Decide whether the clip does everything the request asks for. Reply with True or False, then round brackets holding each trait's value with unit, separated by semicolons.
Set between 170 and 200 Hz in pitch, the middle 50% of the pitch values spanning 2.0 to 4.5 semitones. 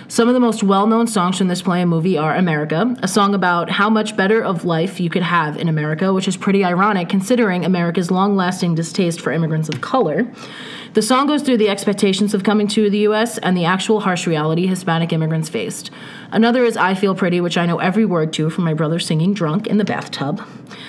True (190 Hz; 3.7 semitones)